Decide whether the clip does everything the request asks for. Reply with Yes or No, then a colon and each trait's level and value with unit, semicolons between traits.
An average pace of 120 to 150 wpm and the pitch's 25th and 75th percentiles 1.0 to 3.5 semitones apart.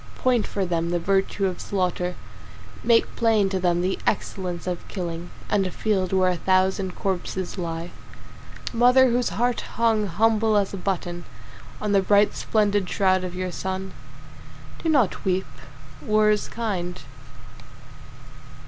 Yes: average, 145 wpm; average, 2.9 semitones